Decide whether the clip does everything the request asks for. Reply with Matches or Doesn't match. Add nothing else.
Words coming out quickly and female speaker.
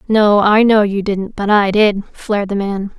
Matches